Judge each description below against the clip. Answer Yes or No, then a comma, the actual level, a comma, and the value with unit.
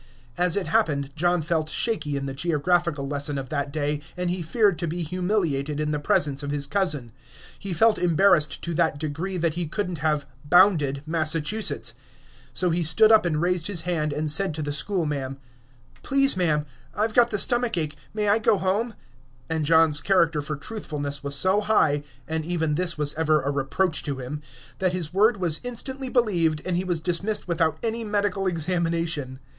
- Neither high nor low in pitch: Yes, medium, 165 Hz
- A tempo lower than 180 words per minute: No, average, 190 wpm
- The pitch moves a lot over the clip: No, average, 4.2 semitones